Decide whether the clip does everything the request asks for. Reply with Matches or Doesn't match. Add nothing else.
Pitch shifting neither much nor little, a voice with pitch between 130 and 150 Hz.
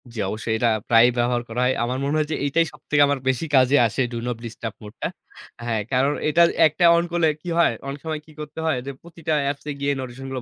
Matches